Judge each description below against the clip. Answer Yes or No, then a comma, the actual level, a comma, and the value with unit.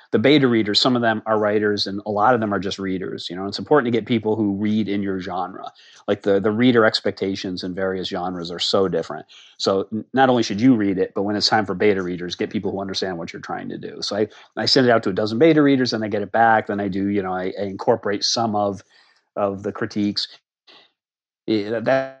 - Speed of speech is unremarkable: No, fast, 255 wpm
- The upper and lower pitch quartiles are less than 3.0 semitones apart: Yes, narrow, 2.6 semitones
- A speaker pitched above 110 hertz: No, low, 105 Hz